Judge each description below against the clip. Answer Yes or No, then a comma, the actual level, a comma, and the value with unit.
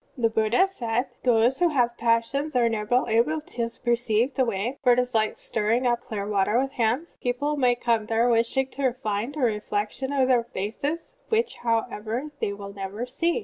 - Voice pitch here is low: No, high, 240 Hz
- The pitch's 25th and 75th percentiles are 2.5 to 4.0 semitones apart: Yes, average, 3.1 semitones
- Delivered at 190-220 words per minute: Yes, average, 200 wpm